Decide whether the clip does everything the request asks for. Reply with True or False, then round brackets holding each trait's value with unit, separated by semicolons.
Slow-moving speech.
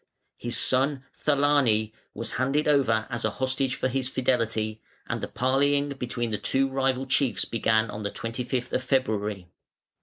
False (155 wpm)